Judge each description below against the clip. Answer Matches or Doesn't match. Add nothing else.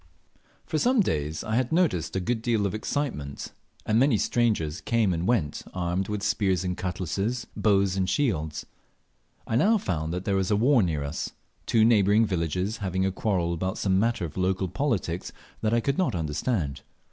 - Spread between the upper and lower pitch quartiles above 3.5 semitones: Matches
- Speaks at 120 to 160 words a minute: Doesn't match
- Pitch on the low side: Matches